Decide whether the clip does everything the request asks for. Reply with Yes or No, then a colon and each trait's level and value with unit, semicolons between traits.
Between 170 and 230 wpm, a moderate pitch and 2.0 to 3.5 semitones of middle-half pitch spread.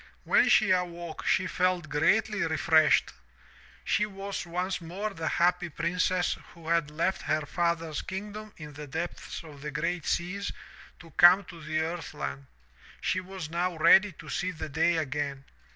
No: average, 160 wpm; medium, 170 Hz; average, 2.8 semitones